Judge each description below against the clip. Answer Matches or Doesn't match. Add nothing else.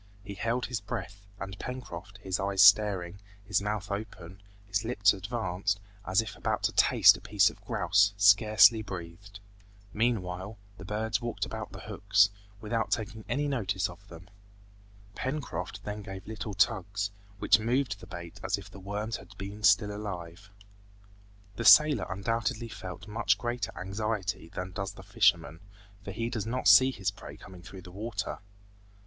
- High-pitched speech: Doesn't match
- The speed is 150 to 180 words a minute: Matches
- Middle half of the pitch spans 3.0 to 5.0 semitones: Doesn't match